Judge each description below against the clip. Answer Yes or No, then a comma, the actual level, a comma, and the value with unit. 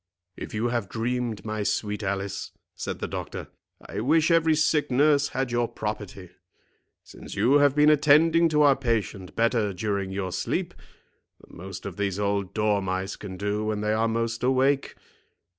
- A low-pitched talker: Yes, low, 110 Hz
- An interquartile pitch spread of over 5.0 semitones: Yes, wide, 5.4 semitones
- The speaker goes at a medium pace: Yes, average, 165 wpm